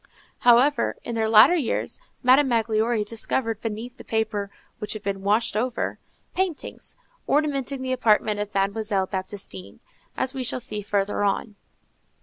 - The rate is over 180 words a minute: No, average, 140 wpm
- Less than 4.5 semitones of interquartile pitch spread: Yes, average, 3.4 semitones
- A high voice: Yes, high, 220 Hz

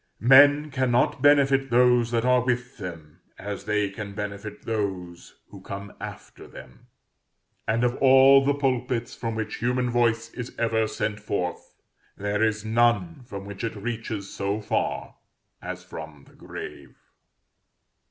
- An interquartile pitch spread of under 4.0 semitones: Yes, average, 3.6 semitones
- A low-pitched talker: Yes, low, 115 Hz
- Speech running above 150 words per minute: No, average, 140 wpm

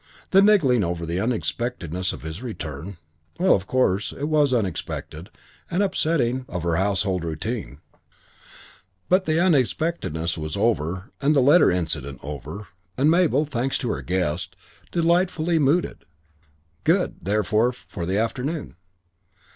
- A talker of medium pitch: No, low, 115 Hz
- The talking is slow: Yes, slow, 130 wpm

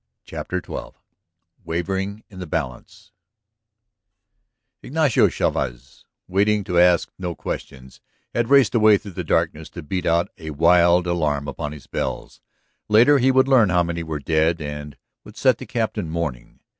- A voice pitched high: No, very low, 85 Hz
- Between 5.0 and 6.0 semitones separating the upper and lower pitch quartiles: Yes, average, 5.3 semitones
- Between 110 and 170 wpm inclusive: Yes, average, 150 wpm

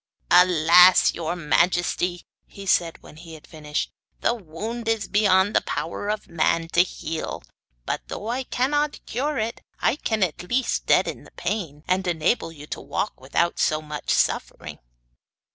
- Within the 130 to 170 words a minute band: Yes, average, 160 wpm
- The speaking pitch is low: No, medium, 180 Hz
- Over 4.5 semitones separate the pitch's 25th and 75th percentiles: Yes, average, 5.0 semitones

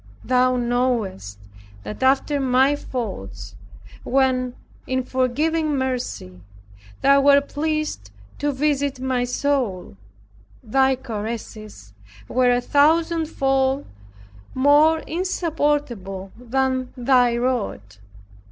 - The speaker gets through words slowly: Yes, slow, 90 wpm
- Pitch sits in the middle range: No, very high, 260 Hz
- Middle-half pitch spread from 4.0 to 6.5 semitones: No, average, 3.1 semitones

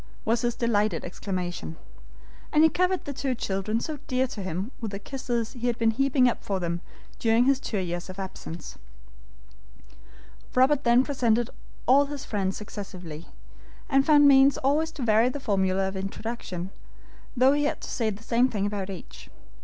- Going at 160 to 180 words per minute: Yes, average, 175 wpm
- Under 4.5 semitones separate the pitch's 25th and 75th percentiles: No, wide, 5.6 semitones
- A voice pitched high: Yes, high, 230 Hz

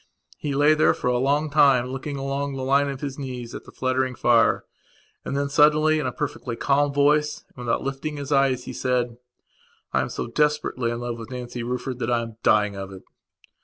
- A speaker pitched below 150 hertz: Yes, low, 135 Hz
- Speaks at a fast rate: Yes, fast, 210 wpm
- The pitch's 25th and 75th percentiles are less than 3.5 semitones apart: Yes, average, 2.7 semitones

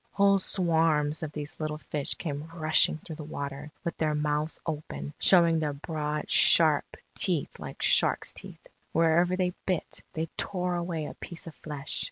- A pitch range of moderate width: No, narrow, 2.3 semitones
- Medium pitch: Yes, medium, 155 Hz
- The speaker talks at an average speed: Yes, average, 165 wpm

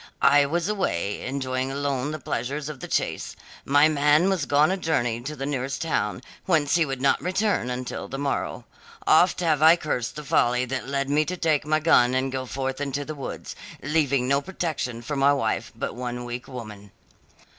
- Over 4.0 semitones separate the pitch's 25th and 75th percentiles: No, average, 3.2 semitones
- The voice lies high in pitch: No, medium, 140 Hz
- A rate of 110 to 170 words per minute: No, average, 195 wpm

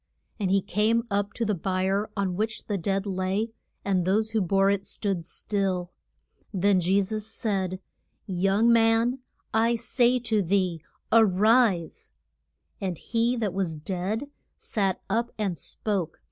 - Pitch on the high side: Yes, high, 200 Hz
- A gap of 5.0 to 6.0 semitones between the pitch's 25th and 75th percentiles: No, average, 2.9 semitones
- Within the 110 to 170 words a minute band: Yes, average, 150 wpm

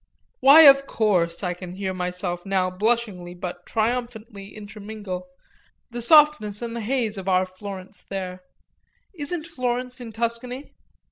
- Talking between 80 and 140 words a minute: Yes, slow, 135 wpm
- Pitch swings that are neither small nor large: Yes, average, 4.8 semitones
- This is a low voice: No, high, 210 Hz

